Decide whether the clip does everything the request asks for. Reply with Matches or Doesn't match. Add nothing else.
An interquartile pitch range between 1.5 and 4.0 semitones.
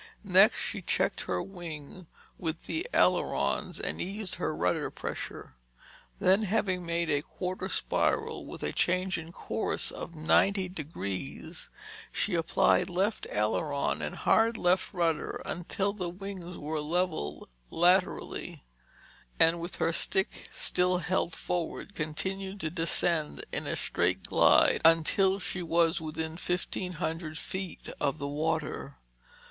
Matches